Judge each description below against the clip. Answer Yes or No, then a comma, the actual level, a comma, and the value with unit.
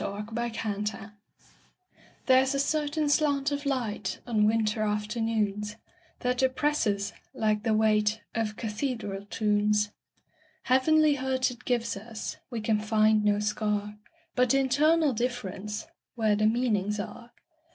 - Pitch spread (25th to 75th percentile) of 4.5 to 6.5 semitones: No, average, 3.8 semitones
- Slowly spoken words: Yes, slow, 105 wpm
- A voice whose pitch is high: Yes, high, 225 Hz